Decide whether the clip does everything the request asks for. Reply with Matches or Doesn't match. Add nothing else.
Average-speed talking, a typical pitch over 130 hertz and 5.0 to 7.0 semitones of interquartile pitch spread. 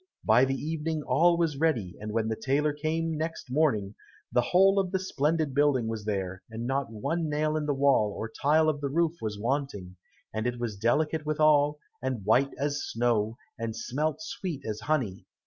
Matches